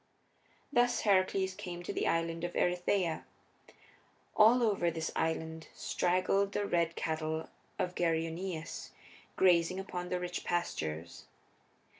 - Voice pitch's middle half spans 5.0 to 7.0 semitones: No, narrow, 2.4 semitones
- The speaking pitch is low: No, medium, 175 Hz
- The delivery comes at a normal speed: No, slow, 115 wpm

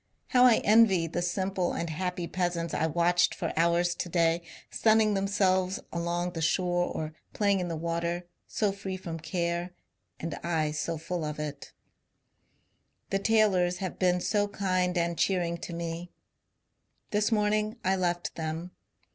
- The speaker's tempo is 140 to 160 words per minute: Yes, average, 155 wpm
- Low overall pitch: No, medium, 175 Hz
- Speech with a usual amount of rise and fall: No, narrow, 2.3 semitones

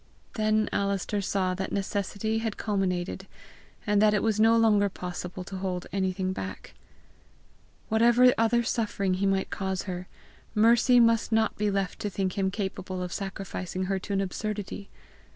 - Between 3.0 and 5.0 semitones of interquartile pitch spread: No, narrow, 2.4 semitones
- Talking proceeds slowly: No, average, 155 wpm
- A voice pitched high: Yes, high, 200 Hz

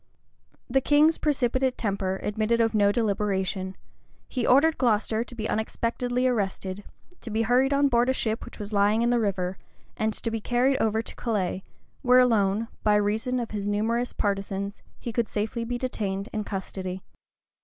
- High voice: Yes, high, 220 Hz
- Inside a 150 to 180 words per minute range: Yes, average, 170 wpm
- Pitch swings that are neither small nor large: Yes, average, 3.2 semitones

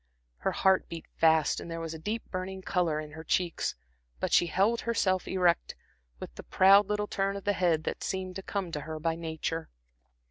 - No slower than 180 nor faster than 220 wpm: Yes, fast, 205 wpm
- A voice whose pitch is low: No, medium, 180 Hz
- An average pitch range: Yes, average, 3.0 semitones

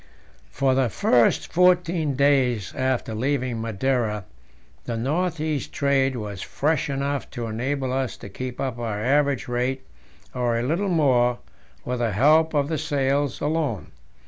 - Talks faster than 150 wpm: No, average, 145 wpm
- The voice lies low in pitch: Yes, low, 130 Hz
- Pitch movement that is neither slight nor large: Yes, average, 3.2 semitones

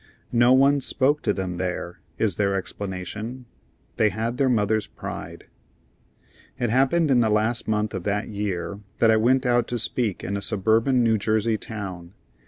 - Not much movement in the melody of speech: No, average, 3.4 semitones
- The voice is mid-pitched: No, low, 110 Hz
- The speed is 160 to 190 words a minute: Yes, average, 170 wpm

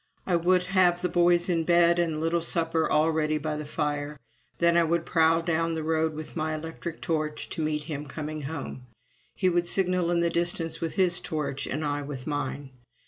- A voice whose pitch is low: No, medium, 160 Hz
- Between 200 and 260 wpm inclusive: Yes, fast, 205 wpm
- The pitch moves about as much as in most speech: No, narrow, 2.1 semitones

